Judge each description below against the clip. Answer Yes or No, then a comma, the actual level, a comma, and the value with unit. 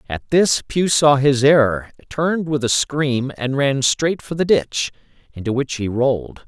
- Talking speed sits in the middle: Yes, average, 185 wpm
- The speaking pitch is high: No, medium, 140 Hz